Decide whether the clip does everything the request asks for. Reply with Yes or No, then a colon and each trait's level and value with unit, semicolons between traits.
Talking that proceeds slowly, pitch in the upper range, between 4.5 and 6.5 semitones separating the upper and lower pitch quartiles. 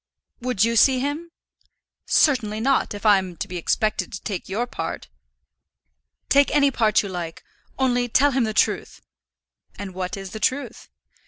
No: average, 165 wpm; high, 220 Hz; average, 5.2 semitones